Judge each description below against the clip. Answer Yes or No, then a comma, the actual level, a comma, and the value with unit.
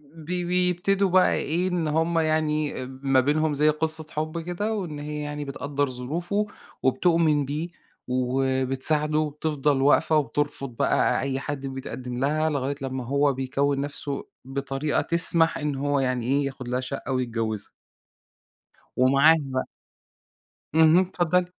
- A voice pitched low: No, medium, 145 Hz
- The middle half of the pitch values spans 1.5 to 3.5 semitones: Yes, average, 3.1 semitones